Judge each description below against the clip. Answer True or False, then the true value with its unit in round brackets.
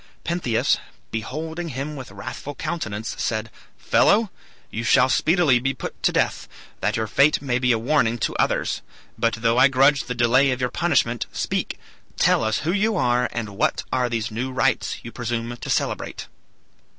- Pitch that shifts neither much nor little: True (3.8 semitones)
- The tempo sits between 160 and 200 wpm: True (175 wpm)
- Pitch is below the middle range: True (125 Hz)